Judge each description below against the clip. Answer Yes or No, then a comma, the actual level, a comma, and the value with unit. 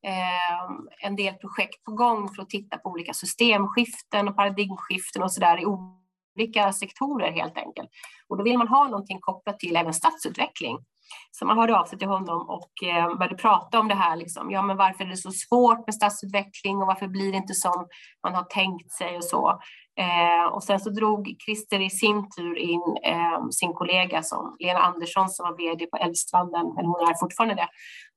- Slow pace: No, average, 190 wpm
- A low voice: No, high, 190 Hz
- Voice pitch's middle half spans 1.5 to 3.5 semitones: Yes, narrow, 2.5 semitones